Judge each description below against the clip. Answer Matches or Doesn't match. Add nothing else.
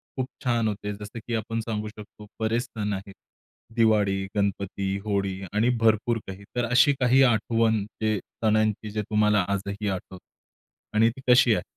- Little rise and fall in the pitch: Matches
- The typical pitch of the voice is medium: Doesn't match